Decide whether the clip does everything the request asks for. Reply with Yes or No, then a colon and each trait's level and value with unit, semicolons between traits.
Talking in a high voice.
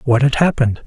No: low, 130 Hz